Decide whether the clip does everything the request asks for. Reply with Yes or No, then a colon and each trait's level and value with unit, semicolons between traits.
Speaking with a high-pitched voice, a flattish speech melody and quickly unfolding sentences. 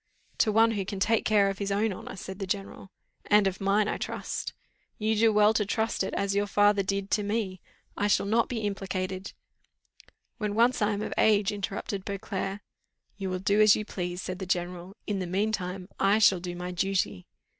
Yes: high, 200 Hz; narrow, 1.9 semitones; fast, 210 wpm